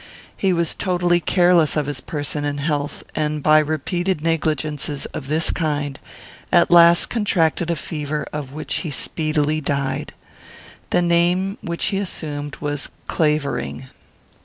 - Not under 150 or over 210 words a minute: No, slow, 135 wpm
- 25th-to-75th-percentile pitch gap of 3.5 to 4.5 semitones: No, average, 2.8 semitones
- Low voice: No, medium, 155 Hz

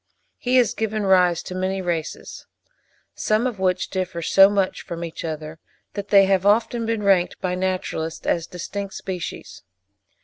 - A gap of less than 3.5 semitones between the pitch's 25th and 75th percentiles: Yes, narrow, 2.5 semitones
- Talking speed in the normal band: Yes, average, 160 wpm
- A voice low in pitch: No, high, 190 Hz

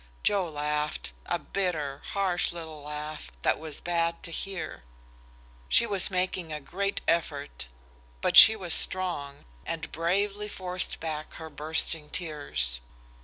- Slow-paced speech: Yes, slow, 130 wpm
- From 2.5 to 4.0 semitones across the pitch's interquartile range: Yes, average, 3.7 semitones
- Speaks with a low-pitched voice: No, medium, 165 Hz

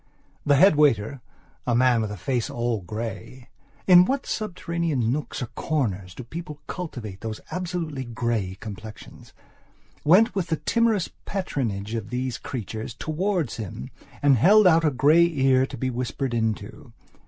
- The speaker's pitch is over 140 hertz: No, low, 130 Hz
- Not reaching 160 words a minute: Yes, average, 140 wpm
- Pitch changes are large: Yes, wide, 6.8 semitones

